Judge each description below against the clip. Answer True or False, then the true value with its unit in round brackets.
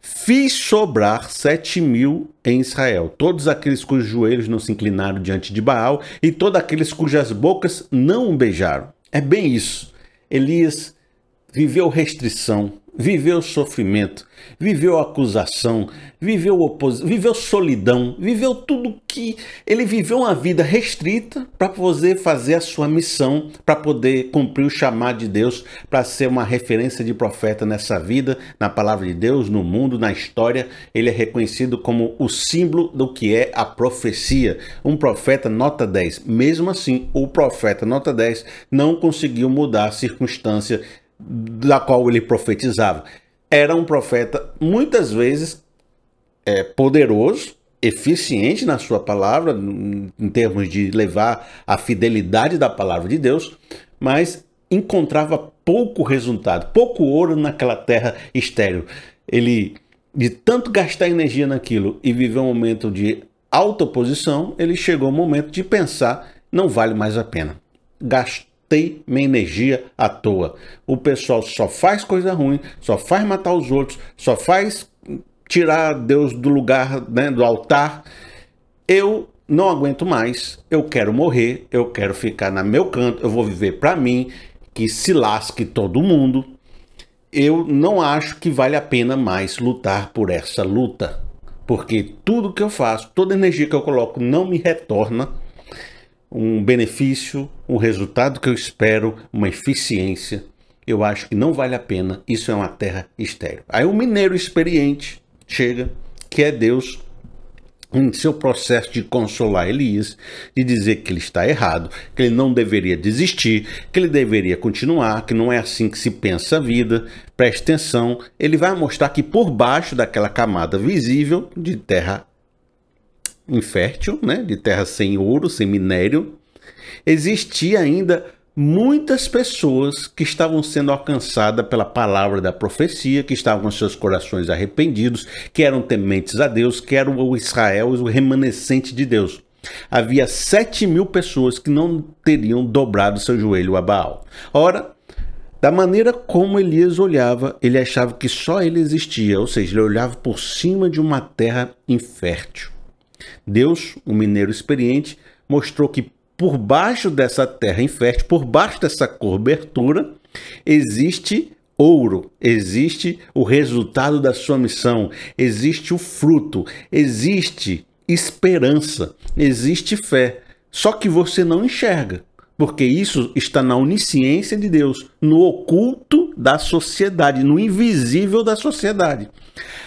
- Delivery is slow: False (145 wpm)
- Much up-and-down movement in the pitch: True (5.9 semitones)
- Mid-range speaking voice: False (130 Hz)